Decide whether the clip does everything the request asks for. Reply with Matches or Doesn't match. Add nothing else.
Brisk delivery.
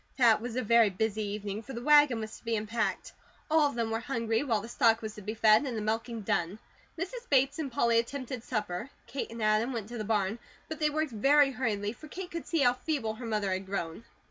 Matches